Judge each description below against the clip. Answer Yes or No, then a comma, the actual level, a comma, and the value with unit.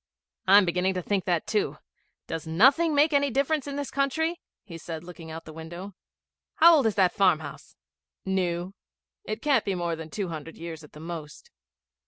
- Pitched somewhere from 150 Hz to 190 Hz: Yes, medium, 185 Hz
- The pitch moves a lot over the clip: Yes, wide, 8.4 semitones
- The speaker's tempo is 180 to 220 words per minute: Yes, average, 190 wpm